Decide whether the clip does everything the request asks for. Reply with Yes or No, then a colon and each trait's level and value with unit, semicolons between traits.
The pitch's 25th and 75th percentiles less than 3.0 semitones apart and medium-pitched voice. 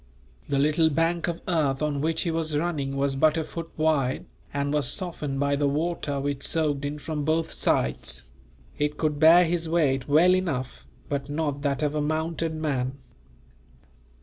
Yes: narrow, 2.4 semitones; medium, 150 Hz